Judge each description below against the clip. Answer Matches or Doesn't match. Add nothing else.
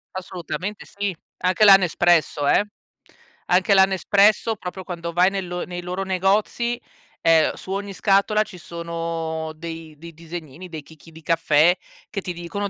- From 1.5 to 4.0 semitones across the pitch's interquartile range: Matches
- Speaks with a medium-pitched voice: Matches